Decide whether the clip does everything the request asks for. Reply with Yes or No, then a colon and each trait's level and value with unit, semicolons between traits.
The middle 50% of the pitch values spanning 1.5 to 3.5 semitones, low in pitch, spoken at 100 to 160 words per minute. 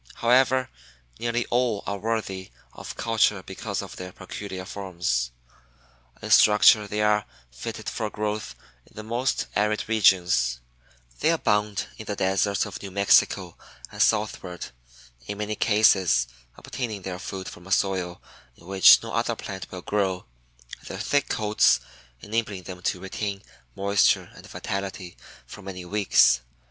Yes: narrow, 2.5 semitones; low, 100 Hz; average, 140 wpm